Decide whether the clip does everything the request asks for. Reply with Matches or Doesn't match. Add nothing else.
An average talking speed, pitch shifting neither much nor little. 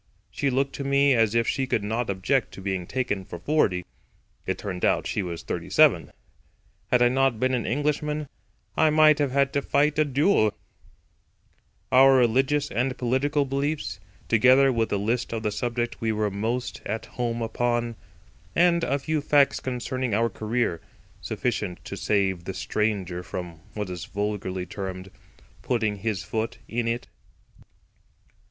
Matches